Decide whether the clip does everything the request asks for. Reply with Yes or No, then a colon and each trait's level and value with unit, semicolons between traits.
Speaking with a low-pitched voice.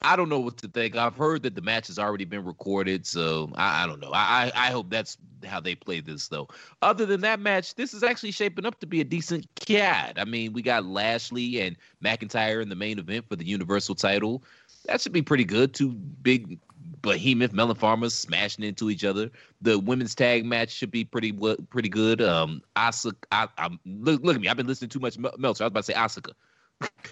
Yes: low, 120 Hz